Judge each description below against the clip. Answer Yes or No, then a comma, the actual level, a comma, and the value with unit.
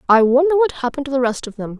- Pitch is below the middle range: No, very high, 265 Hz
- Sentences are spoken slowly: No, fast, 300 wpm